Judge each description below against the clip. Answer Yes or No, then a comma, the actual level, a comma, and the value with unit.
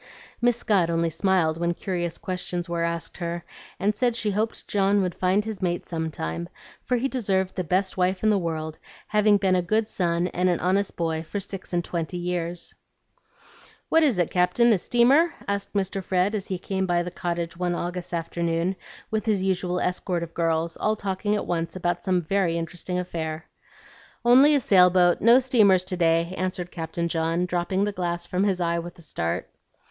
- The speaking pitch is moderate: Yes, medium, 180 Hz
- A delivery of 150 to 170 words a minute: No, average, 195 wpm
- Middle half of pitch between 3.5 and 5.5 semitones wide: No, average, 2.8 semitones